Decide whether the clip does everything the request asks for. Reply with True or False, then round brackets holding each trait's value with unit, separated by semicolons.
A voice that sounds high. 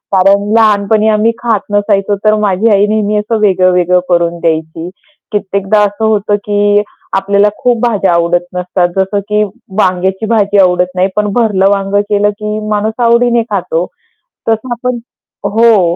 True (205 Hz)